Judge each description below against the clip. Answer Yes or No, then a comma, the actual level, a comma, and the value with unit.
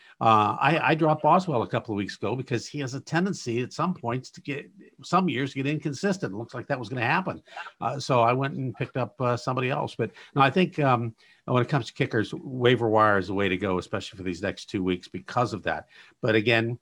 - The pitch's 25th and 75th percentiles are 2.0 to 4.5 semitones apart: Yes, average, 4.0 semitones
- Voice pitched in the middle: No, low, 125 Hz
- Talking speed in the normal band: No, fast, 250 wpm